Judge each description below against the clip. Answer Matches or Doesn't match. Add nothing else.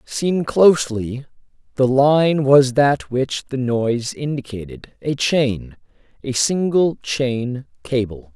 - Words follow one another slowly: Matches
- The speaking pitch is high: Doesn't match